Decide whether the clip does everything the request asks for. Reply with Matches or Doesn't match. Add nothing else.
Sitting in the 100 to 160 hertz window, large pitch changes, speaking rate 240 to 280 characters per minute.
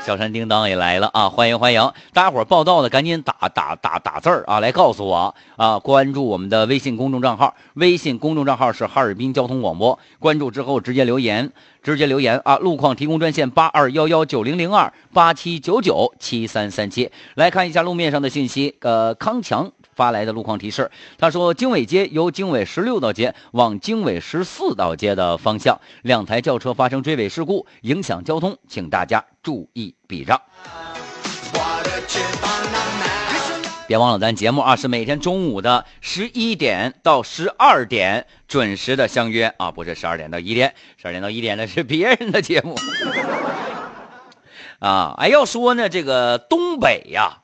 Matches